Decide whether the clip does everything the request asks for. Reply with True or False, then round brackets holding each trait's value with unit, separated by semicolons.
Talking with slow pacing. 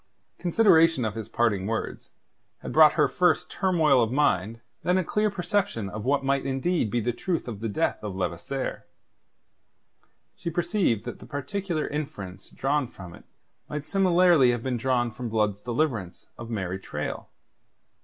False (160 wpm)